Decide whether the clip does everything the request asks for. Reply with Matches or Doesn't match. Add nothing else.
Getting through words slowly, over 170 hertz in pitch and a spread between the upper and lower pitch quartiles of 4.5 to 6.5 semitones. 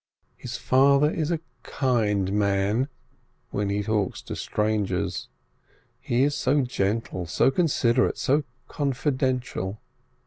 Doesn't match